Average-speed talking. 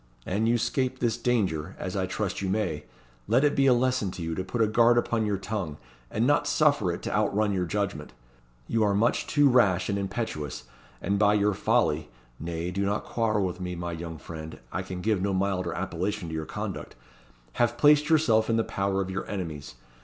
No: fast, 215 wpm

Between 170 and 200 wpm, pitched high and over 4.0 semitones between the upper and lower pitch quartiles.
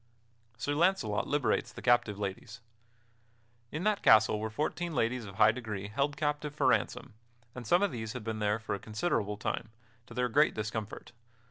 No: average, 180 wpm; low, 115 Hz; average, 5.3 semitones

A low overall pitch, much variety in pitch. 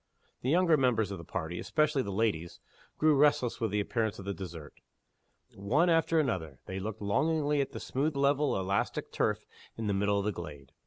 Yes: low, 110 Hz; wide, 7.0 semitones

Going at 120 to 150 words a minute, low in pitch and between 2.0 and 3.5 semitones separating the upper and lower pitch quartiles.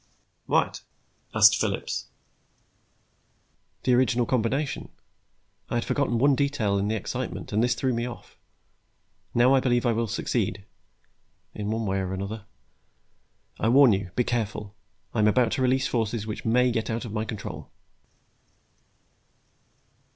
Yes: average, 145 wpm; low, 115 Hz; average, 2.8 semitones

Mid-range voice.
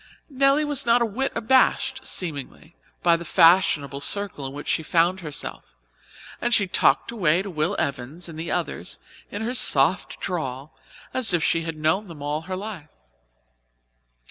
Yes: medium, 175 Hz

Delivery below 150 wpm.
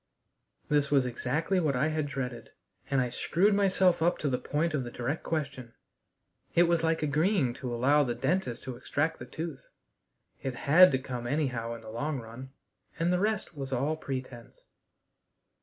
No: average, 175 wpm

